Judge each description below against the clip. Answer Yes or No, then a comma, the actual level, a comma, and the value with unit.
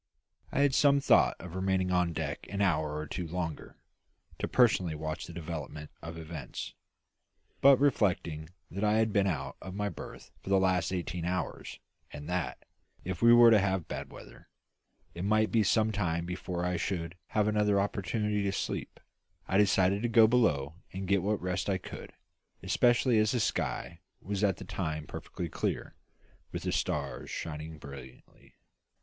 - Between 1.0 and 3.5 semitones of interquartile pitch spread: No, average, 4.1 semitones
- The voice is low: Yes, very low, 95 Hz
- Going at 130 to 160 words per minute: No, average, 170 wpm